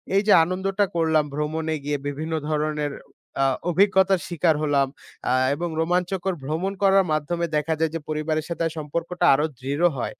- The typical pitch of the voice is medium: Yes, medium, 160 Hz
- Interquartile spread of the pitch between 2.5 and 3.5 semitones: Yes, average, 2.9 semitones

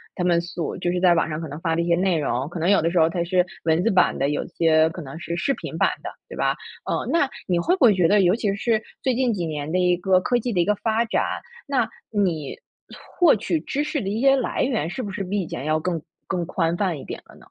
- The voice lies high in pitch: No, medium, 180 Hz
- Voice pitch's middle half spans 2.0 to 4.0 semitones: No, average, 4.4 semitones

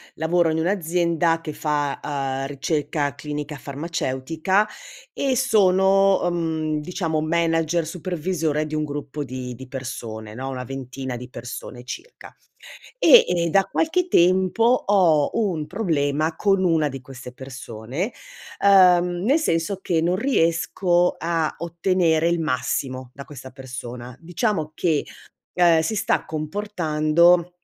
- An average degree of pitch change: Yes, average, 4.3 semitones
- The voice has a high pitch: No, medium, 160 Hz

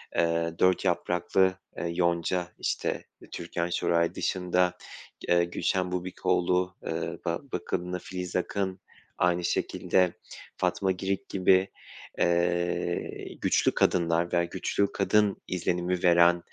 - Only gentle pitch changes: Yes, narrow, 1.1 semitones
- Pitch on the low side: Yes, very low, 90 Hz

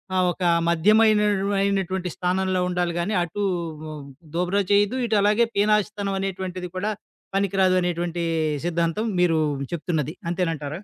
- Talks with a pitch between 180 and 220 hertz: Yes, medium, 185 Hz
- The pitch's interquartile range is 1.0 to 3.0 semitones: Yes, average, 2.7 semitones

